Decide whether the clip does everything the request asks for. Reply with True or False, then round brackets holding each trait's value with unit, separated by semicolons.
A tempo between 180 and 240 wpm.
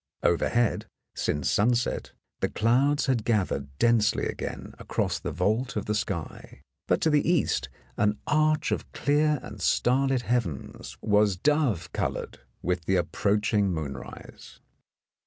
False (135 wpm)